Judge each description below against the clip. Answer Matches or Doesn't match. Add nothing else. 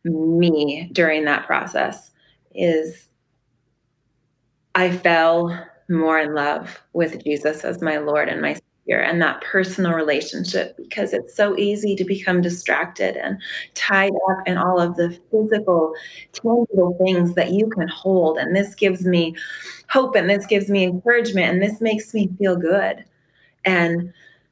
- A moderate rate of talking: Matches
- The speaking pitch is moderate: Matches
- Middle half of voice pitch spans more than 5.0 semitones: Doesn't match